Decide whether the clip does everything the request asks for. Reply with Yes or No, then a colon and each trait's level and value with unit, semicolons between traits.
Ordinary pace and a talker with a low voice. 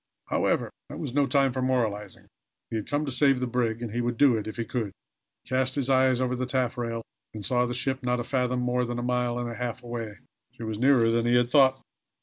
No: fast, 250 wpm; low, 125 Hz